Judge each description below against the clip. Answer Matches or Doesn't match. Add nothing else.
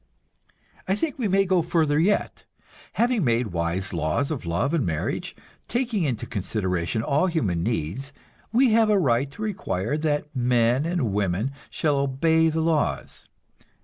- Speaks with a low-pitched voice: Doesn't match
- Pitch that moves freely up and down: Matches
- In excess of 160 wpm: Doesn't match